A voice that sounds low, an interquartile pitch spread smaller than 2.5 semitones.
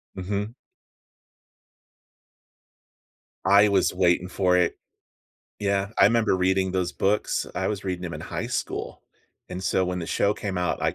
Yes: very low, 95 Hz; narrow, 1.8 semitones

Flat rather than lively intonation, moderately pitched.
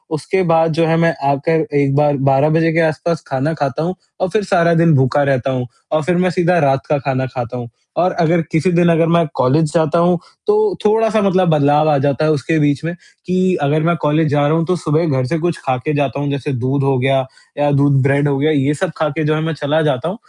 No: average, 3.1 semitones; medium, 155 Hz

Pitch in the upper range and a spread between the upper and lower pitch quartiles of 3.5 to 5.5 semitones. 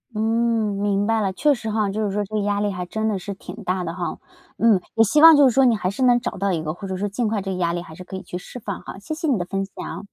No: high, 205 Hz; average, 3.1 semitones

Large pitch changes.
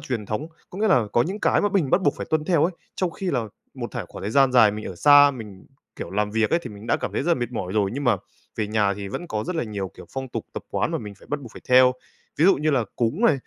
Yes: wide, 6.3 semitones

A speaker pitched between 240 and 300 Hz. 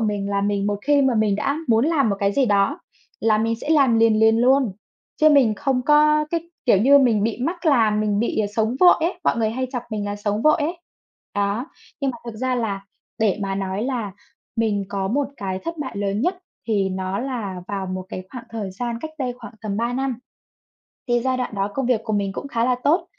No: high, 225 Hz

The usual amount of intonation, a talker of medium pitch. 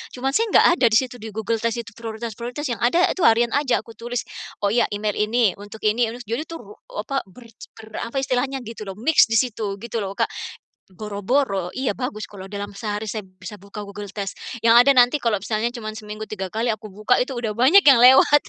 No: average, 3.1 semitones; high, 225 Hz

